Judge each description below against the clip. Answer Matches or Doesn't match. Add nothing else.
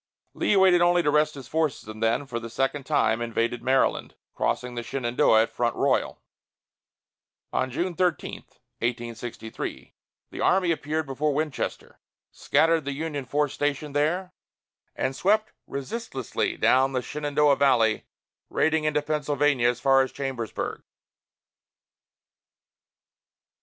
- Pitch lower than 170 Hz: Matches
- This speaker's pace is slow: Matches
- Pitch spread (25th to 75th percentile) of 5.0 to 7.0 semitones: Doesn't match